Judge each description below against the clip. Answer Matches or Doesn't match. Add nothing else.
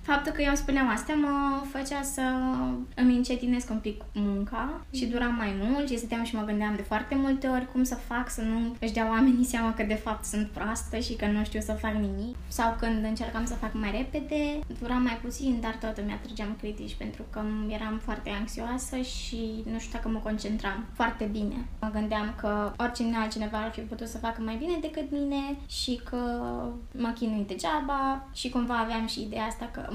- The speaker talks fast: Matches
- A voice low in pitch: Doesn't match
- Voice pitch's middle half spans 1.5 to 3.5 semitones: Matches